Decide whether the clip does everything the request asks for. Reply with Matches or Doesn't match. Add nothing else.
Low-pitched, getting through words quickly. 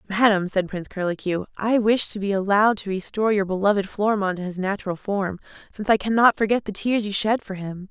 Doesn't match